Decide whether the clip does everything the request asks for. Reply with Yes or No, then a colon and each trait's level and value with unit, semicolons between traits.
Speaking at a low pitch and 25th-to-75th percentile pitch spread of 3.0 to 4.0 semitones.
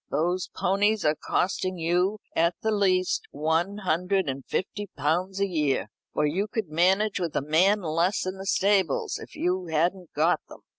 No: medium, 180 Hz; average, 3.3 semitones